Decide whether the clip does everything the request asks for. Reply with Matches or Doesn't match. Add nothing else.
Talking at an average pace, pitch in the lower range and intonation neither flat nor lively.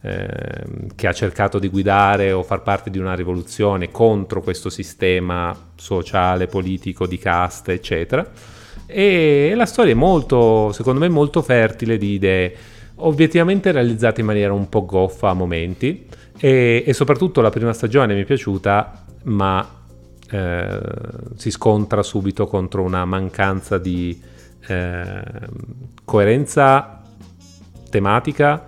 Matches